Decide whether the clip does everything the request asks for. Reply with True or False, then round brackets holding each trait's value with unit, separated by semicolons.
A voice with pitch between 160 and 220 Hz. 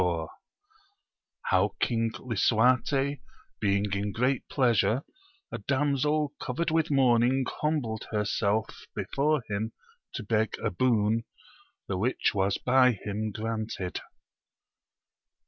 False (115 Hz)